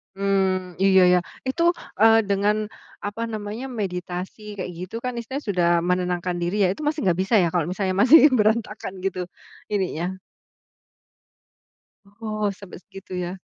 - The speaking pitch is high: Yes, high, 195 Hz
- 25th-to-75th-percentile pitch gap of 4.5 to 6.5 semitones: No, average, 2.8 semitones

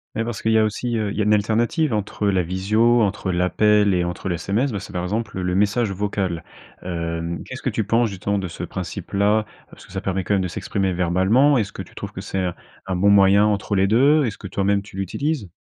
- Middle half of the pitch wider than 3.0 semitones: No, average, 2.7 semitones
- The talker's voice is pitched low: Yes, low, 100 Hz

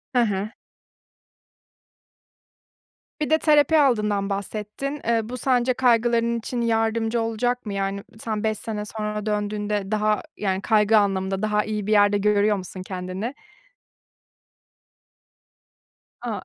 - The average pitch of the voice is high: Yes, high, 215 Hz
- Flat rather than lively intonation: Yes, narrow, 2.3 semitones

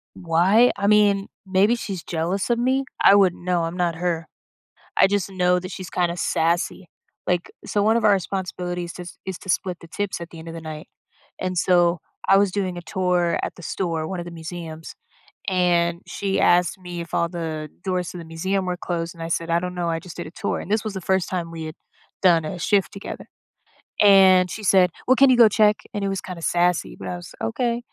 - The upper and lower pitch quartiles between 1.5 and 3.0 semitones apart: Yes, narrow, 2.5 semitones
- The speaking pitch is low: No, medium, 180 Hz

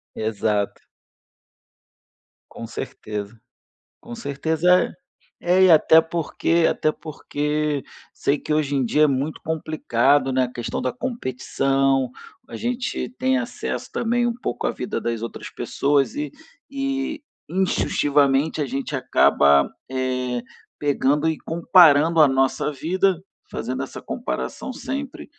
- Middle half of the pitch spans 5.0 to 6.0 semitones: Yes, wide, 5.4 semitones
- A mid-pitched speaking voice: Yes, medium, 150 Hz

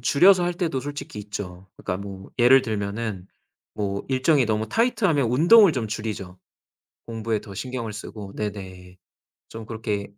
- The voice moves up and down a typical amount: Yes, average, 4.8 semitones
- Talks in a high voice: No, low, 110 Hz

